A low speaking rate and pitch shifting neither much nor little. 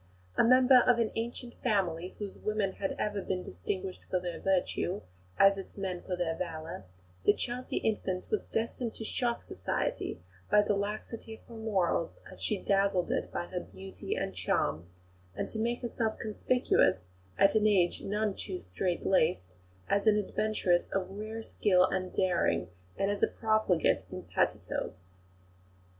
No: average, 160 wpm; average, 3.3 semitones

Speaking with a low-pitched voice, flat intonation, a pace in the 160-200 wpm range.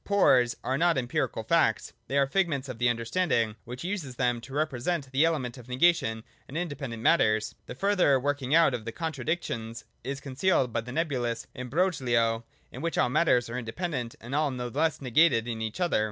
No: low, 130 Hz; average, 5.1 semitones; average, 195 wpm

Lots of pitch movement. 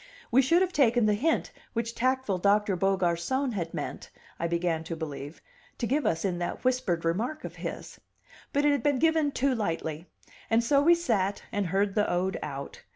Yes: wide, 7.2 semitones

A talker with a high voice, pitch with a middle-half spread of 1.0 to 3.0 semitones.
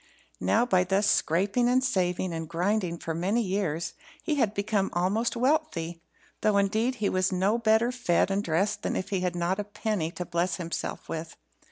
No: high, 195 Hz; average, 3.9 semitones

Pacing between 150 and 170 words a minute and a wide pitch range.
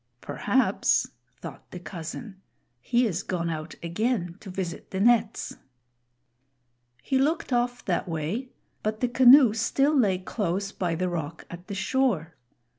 No: average, 140 wpm; wide, 5.9 semitones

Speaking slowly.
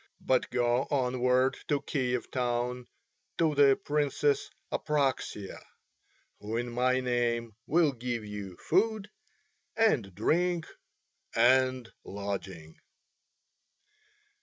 Yes: slow, 90 wpm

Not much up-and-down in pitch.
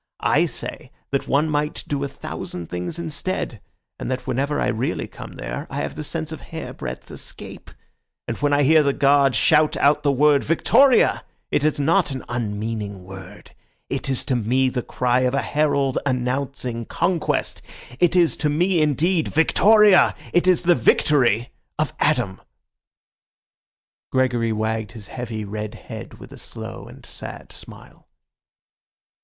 No: average, 4.7 semitones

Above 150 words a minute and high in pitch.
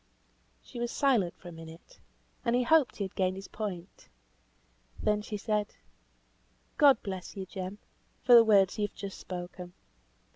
Yes: average, 160 wpm; high, 200 Hz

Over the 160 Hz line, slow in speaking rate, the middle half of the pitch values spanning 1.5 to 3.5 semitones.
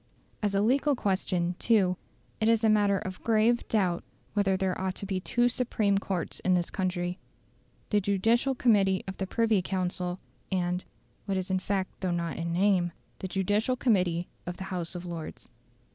No: high, 190 Hz; average, 175 wpm; average, 2.7 semitones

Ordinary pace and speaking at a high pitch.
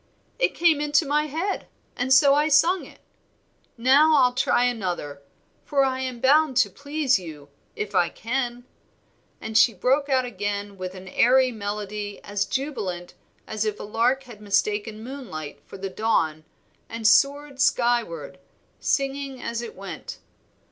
Yes: average, 150 wpm; high, 240 Hz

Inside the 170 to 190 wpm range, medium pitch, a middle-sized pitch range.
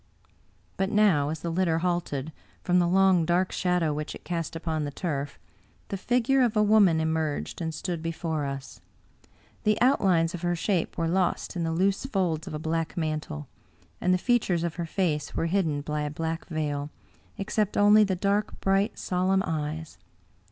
Yes: average, 180 wpm; medium, 170 Hz; average, 3.4 semitones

